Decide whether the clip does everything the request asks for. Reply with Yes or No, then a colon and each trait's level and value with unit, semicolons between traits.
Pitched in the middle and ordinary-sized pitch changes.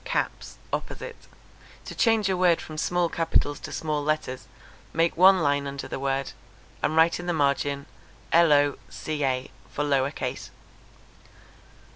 Yes: medium, 150 Hz; average, 3.4 semitones